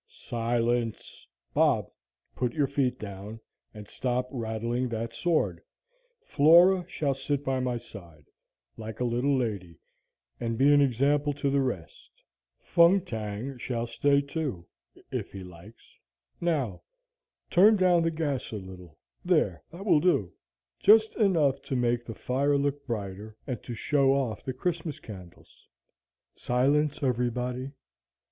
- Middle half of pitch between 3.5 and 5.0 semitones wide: Yes, average, 4.4 semitones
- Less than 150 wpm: Yes, slow, 135 wpm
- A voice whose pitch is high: No, low, 125 Hz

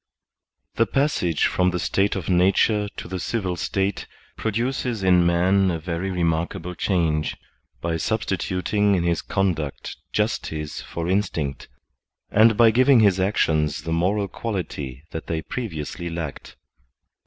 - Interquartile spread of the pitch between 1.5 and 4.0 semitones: Yes, average, 3.7 semitones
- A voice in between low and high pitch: No, very low, 90 Hz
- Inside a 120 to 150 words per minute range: Yes, slow, 135 wpm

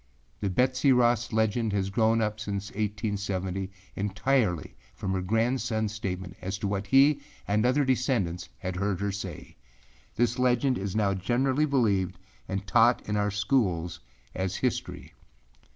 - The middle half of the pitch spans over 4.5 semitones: No, average, 4.0 semitones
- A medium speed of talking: Yes, average, 145 wpm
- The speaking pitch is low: Yes, low, 105 Hz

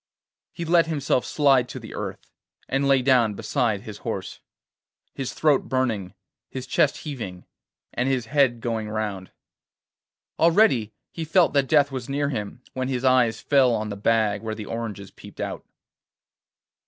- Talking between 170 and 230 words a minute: No, average, 155 wpm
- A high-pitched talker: No, low, 125 Hz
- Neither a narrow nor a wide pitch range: Yes, average, 4.3 semitones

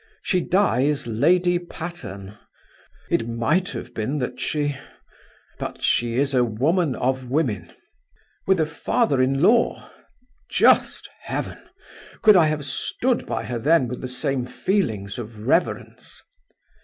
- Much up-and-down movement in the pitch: Yes, wide, 6.3 semitones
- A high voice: No, low, 135 Hz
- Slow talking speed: Yes, slow, 130 wpm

